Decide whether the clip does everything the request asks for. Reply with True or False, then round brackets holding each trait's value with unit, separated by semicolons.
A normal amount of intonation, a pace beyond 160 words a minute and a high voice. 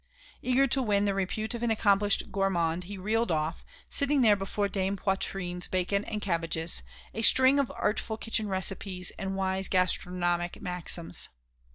False (3.1 semitones; 155 wpm; 195 Hz)